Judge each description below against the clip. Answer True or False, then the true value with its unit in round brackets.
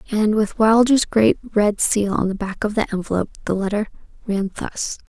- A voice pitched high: True (210 Hz)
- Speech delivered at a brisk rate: False (190 wpm)